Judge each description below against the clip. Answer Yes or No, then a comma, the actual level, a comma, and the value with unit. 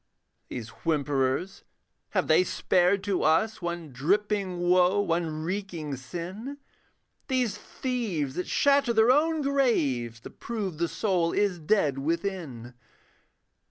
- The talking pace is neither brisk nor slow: No, slow, 120 wpm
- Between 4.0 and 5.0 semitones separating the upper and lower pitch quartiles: No, wide, 5.4 semitones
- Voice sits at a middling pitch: Yes, medium, 180 Hz